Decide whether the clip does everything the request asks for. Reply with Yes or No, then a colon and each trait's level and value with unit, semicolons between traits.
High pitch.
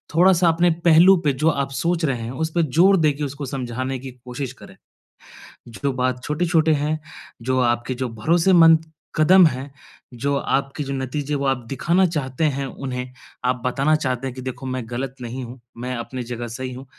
No: low, 135 Hz